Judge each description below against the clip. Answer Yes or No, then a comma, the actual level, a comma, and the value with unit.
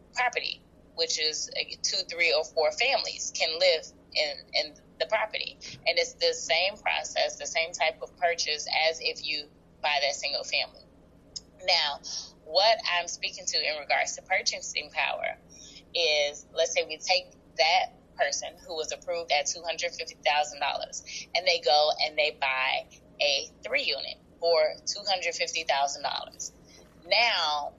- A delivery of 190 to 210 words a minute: No, average, 140 wpm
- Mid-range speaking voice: Yes, medium, 170 Hz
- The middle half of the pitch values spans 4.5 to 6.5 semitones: Yes, average, 4.9 semitones